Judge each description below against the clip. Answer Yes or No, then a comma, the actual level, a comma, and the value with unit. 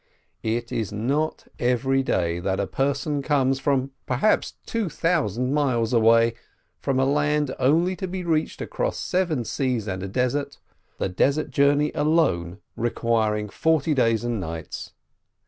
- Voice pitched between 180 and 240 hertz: No, low, 130 Hz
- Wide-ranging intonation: No, average, 4.6 semitones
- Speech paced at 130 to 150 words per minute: Yes, average, 145 wpm